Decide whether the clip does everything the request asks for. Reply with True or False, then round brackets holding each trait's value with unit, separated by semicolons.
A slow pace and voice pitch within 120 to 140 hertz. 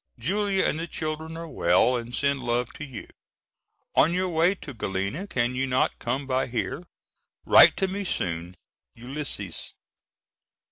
False (150 wpm; 135 Hz)